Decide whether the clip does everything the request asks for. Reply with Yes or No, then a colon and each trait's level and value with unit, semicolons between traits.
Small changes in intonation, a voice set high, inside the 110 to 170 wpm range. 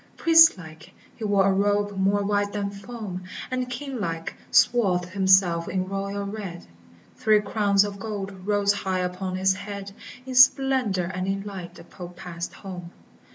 Yes: narrow, 1.9 semitones; high, 200 Hz; average, 160 wpm